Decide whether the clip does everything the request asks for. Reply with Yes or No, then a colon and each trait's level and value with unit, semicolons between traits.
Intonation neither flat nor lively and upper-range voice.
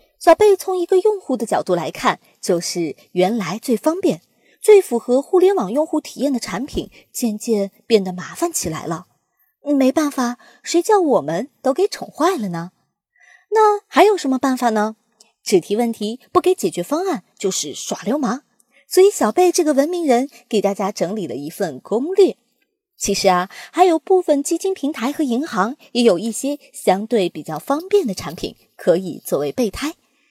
No: wide, 8.5 semitones; very high, 260 Hz